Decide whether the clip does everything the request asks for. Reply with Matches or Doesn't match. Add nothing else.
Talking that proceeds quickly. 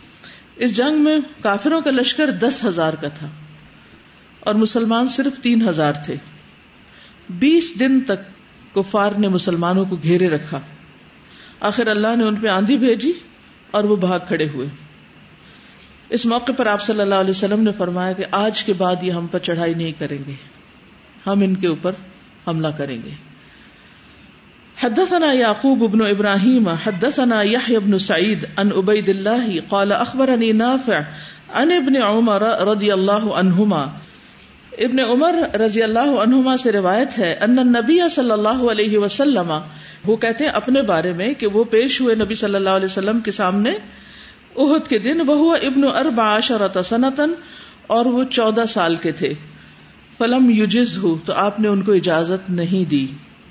Doesn't match